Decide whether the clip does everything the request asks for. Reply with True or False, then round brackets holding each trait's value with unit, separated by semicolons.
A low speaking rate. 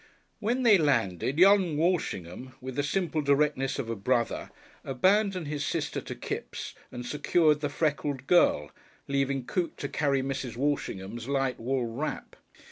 False (145 wpm)